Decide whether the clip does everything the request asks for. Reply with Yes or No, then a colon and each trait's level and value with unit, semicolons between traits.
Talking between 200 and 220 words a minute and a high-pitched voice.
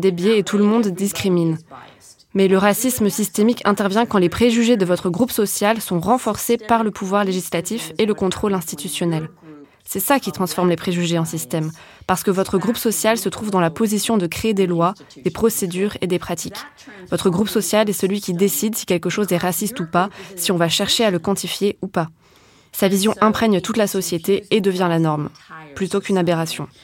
Yes: average, 205 wpm; high, 195 Hz